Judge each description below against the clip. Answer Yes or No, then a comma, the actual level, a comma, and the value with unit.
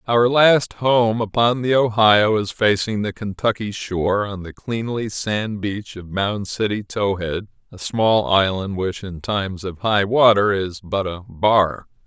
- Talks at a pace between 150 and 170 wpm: Yes, average, 165 wpm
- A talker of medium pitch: No, low, 105 Hz